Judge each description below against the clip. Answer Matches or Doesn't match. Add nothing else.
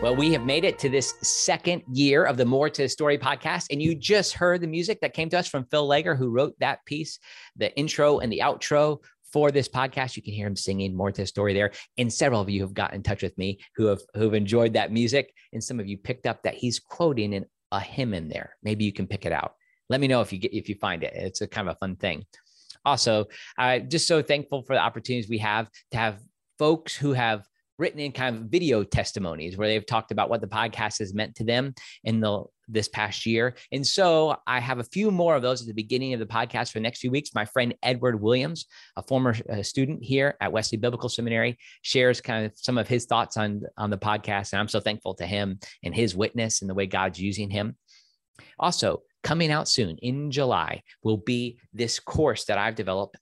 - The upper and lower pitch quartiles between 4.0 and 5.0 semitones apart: Matches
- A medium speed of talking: Doesn't match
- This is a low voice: Matches